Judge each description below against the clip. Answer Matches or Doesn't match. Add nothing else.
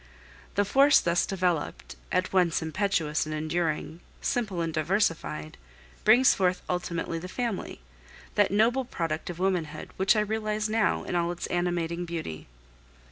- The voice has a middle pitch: Matches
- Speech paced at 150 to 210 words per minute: Doesn't match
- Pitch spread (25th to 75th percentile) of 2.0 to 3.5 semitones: Doesn't match